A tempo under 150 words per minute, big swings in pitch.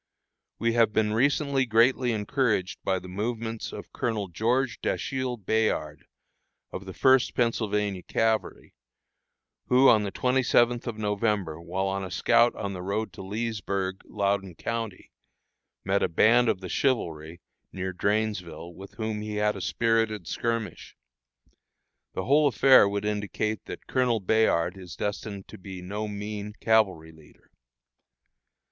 No: average, 140 wpm; average, 3.2 semitones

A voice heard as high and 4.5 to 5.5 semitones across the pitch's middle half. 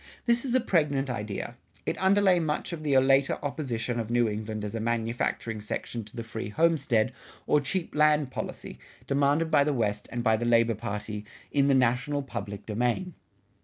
No: low, 125 Hz; average, 5.0 semitones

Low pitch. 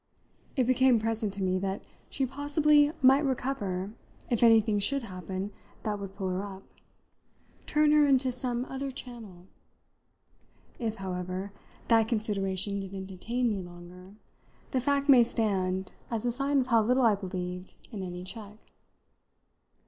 No: high, 215 Hz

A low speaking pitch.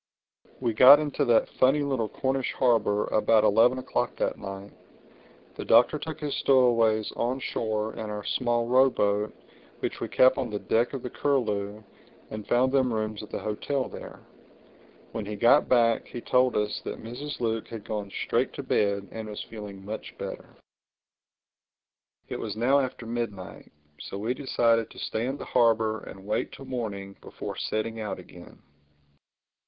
Yes: low, 115 Hz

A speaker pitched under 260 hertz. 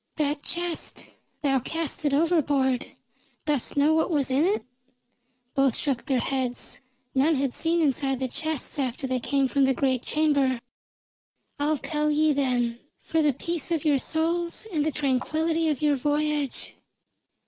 No: very high, 290 Hz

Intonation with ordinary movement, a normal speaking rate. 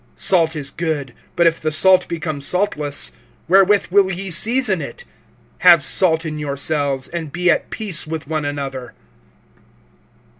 Yes: average, 4.0 semitones; average, 145 wpm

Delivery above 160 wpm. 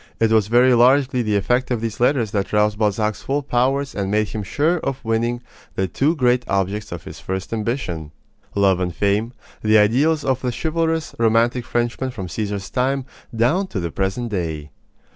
Yes: average, 180 wpm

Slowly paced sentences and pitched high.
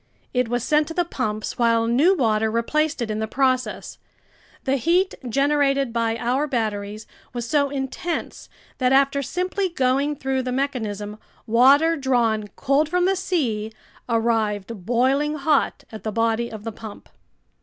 No: average, 155 wpm; very high, 255 Hz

